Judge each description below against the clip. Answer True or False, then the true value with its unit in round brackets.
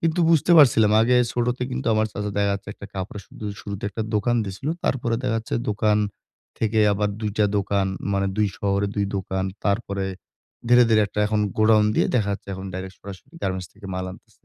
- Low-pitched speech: True (105 Hz)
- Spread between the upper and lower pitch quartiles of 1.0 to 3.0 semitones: True (2.4 semitones)